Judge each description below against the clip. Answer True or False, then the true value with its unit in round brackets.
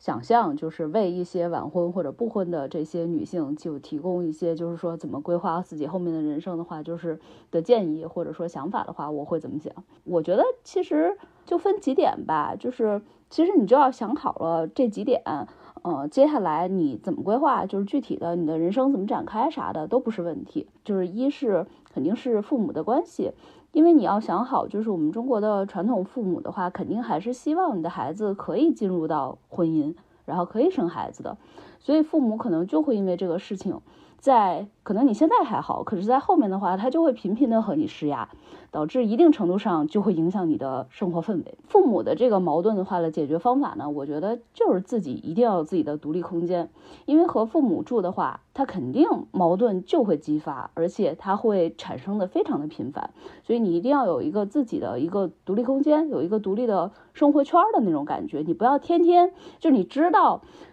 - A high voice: True (205 Hz)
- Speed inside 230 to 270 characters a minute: False (320 characters per minute)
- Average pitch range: False (8.6 semitones)